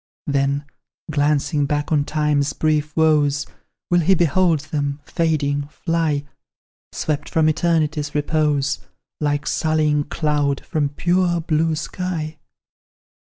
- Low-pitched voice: No, medium, 150 Hz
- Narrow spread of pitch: Yes, narrow, 1.7 semitones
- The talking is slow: Yes, slow, 110 wpm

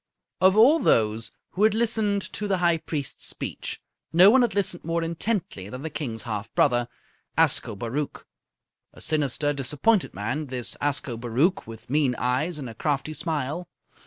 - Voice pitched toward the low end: No, medium, 150 Hz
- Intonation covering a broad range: Yes, wide, 6.8 semitones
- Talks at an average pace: Yes, average, 150 wpm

